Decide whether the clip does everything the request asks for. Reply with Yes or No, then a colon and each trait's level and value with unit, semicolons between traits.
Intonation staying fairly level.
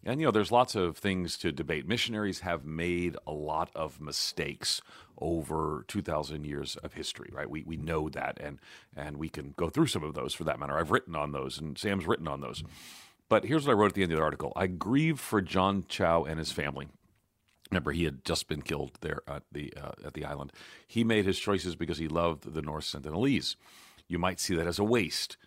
No: average, 4.4 semitones